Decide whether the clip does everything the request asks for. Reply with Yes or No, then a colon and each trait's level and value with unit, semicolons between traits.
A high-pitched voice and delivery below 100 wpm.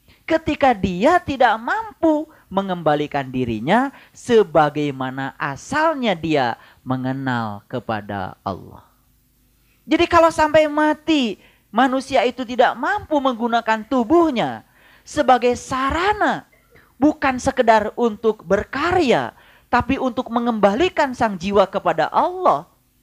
Yes: high, 245 Hz; average, 90 wpm